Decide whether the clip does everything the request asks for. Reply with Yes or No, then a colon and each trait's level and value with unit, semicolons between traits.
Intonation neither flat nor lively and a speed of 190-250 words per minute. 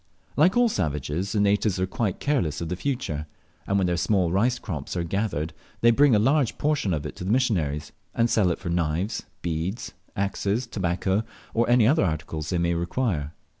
No: wide, 5.7 semitones; average, 195 wpm